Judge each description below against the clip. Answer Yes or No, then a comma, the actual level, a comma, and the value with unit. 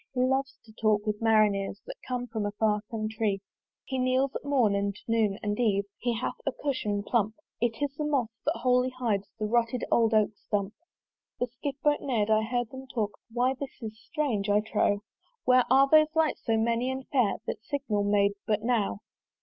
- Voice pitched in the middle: No, high, 230 Hz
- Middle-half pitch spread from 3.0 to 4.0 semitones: Yes, average, 3.5 semitones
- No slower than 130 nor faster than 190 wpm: No, average, 200 wpm